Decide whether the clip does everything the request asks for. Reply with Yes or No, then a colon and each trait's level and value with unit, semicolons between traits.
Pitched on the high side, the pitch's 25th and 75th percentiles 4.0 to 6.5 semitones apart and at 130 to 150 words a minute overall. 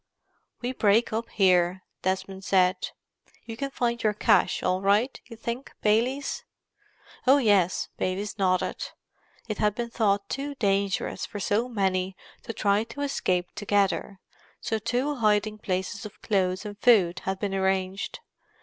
No: high, 205 Hz; average, 3.3 semitones; average, 145 wpm